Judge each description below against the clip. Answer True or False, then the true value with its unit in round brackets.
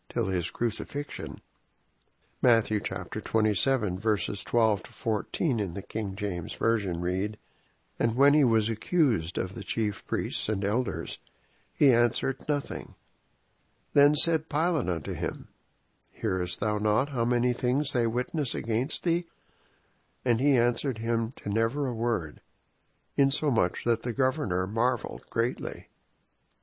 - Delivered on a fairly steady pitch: False (4.5 semitones)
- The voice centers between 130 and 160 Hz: False (115 Hz)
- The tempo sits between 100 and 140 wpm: True (135 wpm)